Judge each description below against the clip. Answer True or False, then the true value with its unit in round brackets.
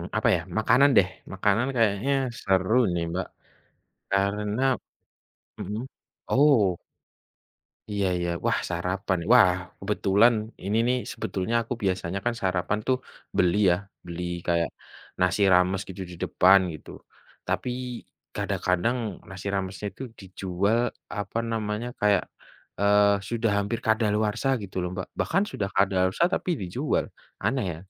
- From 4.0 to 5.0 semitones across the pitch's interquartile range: False (2.9 semitones)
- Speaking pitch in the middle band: False (100 Hz)